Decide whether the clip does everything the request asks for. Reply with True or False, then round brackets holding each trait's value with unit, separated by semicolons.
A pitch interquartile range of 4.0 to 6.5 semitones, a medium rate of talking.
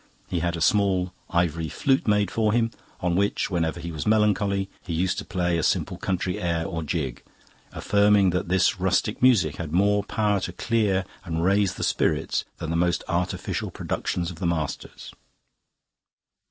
False (3.2 semitones; 170 wpm)